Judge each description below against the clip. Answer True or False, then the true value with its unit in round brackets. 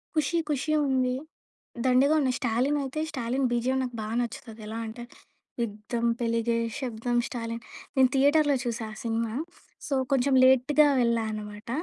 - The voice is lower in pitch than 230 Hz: False (245 Hz)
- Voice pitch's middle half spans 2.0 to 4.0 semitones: True (2.6 semitones)